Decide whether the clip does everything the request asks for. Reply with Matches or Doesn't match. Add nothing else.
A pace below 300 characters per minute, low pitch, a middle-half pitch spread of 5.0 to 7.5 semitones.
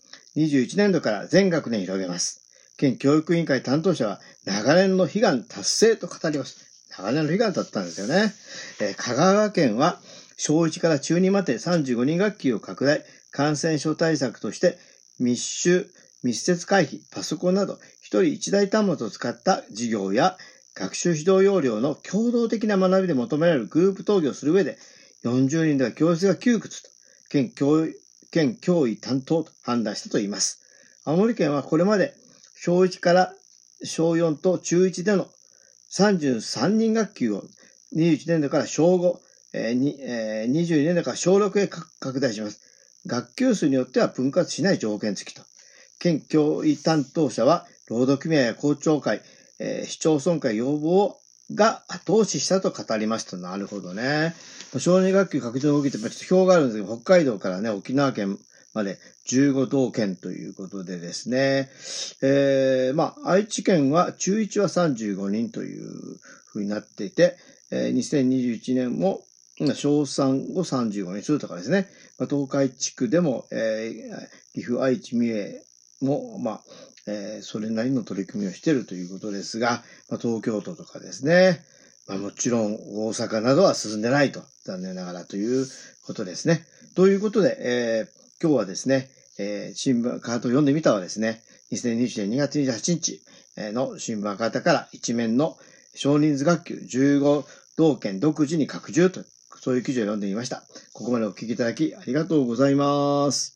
Doesn't match